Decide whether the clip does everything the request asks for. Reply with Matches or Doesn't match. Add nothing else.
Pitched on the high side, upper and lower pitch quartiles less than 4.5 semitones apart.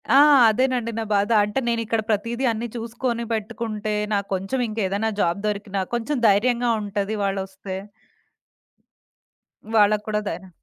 Matches